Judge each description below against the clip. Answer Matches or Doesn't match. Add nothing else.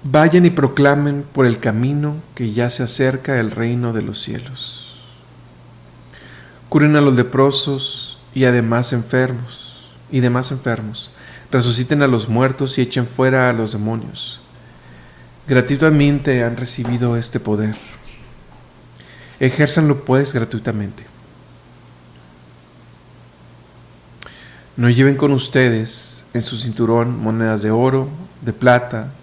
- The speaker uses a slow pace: Matches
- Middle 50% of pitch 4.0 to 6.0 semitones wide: Doesn't match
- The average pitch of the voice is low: Matches